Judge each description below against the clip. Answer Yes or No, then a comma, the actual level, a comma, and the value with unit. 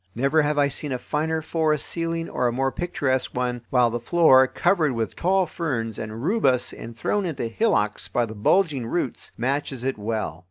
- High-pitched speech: No, low, 135 Hz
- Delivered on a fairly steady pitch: No, average, 5.3 semitones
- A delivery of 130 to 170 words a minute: No, average, 190 wpm